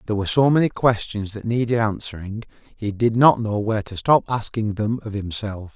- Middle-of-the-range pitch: No, low, 110 Hz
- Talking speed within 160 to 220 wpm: Yes, average, 200 wpm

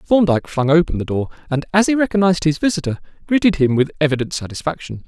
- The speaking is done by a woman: No, male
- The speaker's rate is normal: Yes, average, 190 wpm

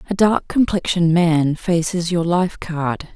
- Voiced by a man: No, female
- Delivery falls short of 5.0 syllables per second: Yes, 4.1 syllables/s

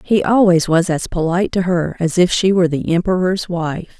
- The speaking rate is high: Yes, fast, 210 wpm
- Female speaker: Yes, female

